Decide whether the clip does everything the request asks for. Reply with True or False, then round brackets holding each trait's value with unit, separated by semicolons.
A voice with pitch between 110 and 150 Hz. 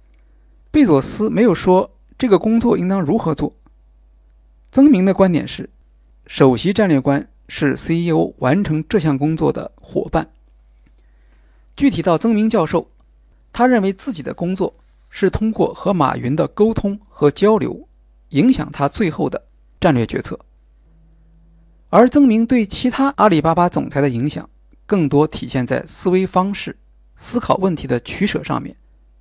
False (165 Hz)